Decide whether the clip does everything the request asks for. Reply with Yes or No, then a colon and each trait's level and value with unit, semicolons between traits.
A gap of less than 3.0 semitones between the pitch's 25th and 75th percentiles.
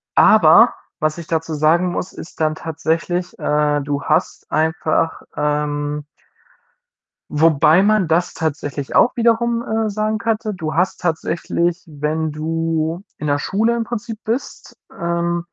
No: average, 3.8 semitones